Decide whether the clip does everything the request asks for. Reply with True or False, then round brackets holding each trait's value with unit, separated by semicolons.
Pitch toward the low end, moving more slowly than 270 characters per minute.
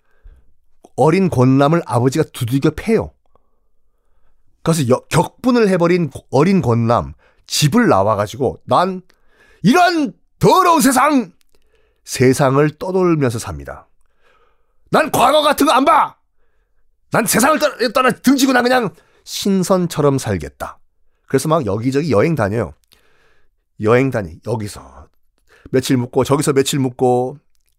False (145 Hz; 240 characters per minute)